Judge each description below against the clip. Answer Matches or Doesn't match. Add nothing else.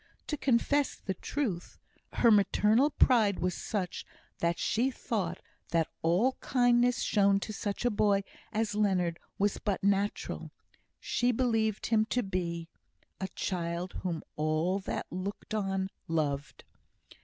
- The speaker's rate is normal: Doesn't match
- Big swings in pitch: Doesn't match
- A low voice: Doesn't match